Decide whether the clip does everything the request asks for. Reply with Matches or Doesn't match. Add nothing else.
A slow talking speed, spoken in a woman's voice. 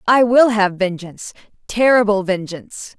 Matches